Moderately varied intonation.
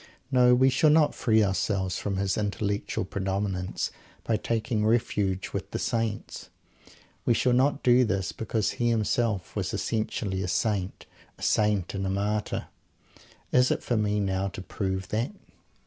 Yes: average, 3.3 semitones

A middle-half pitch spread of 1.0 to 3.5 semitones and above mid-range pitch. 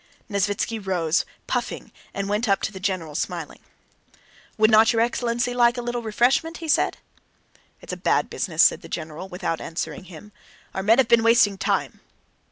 No: average, 4.0 semitones; high, 210 Hz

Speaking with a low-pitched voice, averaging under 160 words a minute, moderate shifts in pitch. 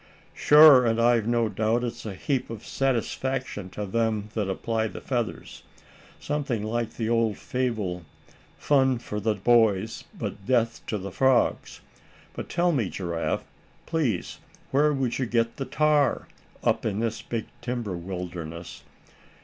Yes: low, 115 Hz; average, 145 wpm; average, 3.5 semitones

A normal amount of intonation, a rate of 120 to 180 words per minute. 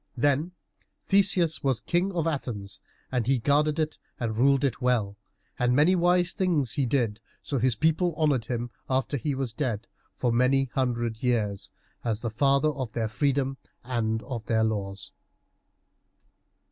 Yes: average, 4.2 semitones; average, 160 wpm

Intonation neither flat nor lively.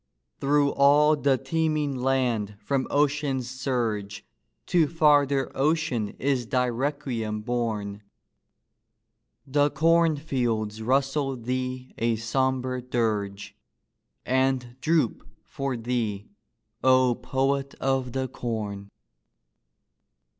Yes: average, 3.1 semitones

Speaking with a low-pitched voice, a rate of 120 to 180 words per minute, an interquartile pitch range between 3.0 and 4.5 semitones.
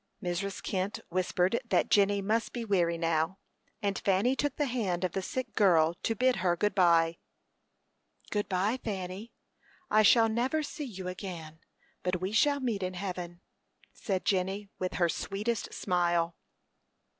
No: high, 190 Hz; average, 155 wpm; average, 3.5 semitones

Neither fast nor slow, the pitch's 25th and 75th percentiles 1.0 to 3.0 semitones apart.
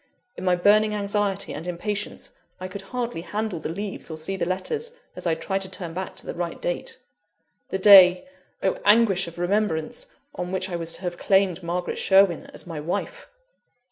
Yes: average, 190 wpm; average, 2.7 semitones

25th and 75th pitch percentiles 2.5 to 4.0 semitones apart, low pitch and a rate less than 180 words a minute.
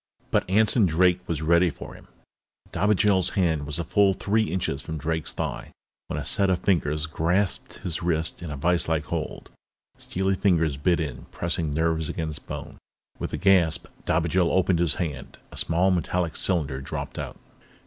Yes: average, 2.8 semitones; very low, 85 Hz; average, 170 wpm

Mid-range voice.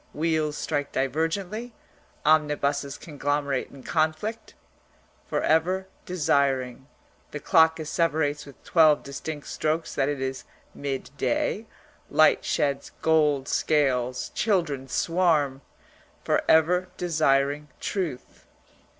Yes: medium, 150 Hz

